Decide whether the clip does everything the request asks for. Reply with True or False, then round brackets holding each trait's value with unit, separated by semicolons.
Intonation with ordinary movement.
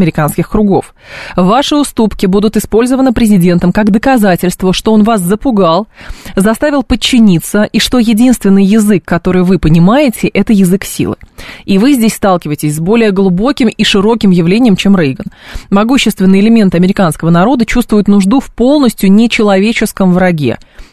True (3.6 semitones)